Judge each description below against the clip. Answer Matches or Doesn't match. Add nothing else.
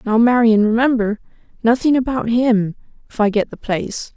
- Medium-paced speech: Matches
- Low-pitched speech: Doesn't match